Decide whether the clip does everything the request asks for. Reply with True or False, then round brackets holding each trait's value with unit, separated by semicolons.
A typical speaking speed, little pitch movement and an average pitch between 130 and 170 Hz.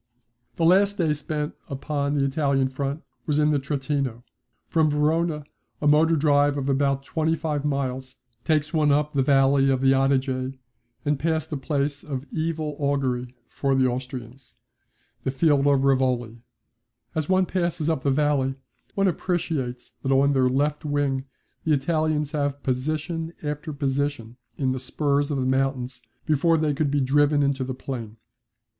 True (160 wpm; 2.3 semitones; 140 Hz)